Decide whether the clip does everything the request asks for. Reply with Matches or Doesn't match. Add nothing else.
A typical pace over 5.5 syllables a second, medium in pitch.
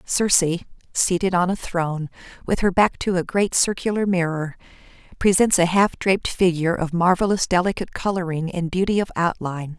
Matches